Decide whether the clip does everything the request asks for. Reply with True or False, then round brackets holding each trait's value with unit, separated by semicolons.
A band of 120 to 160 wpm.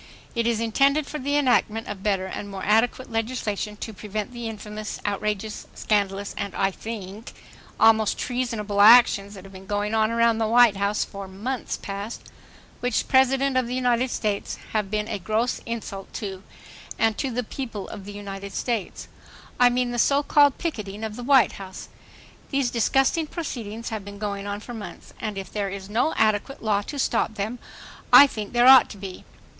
False (185 wpm)